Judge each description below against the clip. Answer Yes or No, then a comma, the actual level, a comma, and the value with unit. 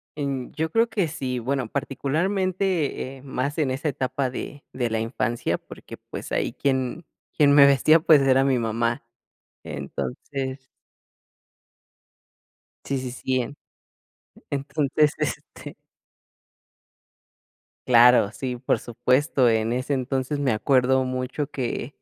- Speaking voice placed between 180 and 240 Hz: No, low, 135 Hz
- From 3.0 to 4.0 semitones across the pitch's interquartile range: No, narrow, 2.4 semitones